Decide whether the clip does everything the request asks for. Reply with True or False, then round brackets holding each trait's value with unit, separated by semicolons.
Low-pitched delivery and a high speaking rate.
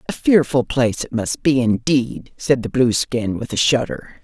False (125 Hz; 185 wpm)